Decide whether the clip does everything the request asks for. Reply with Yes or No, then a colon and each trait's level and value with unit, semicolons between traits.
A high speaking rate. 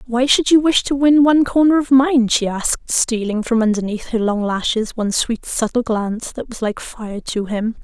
Yes: fast, 215 wpm